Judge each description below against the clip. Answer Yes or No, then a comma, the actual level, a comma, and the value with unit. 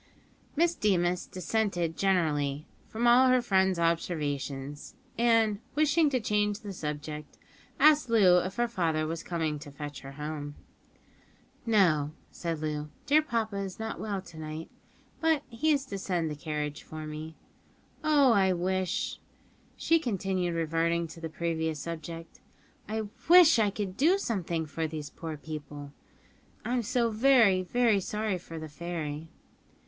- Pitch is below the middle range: No, medium, 180 Hz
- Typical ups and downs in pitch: No, wide, 6.1 semitones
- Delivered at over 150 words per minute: No, average, 145 wpm